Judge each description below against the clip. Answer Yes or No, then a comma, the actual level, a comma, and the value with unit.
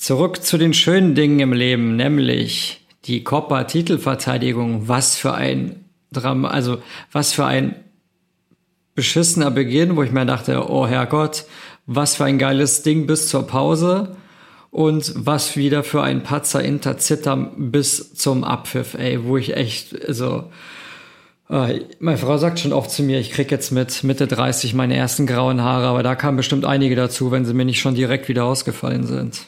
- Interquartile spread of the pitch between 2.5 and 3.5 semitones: Yes, average, 3.0 semitones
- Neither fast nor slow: Yes, average, 165 wpm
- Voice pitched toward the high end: No, low, 135 Hz